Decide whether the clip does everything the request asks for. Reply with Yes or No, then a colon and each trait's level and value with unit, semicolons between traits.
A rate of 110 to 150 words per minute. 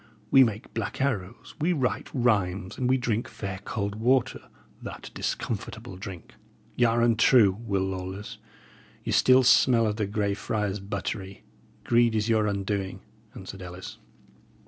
Yes: average, 145 wpm